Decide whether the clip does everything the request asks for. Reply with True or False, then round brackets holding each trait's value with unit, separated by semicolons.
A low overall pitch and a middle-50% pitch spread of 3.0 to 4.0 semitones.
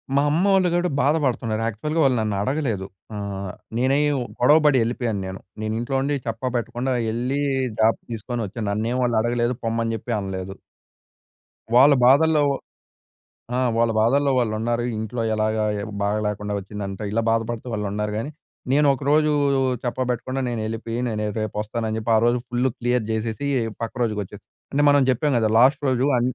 True (120 Hz; 3.4 semitones)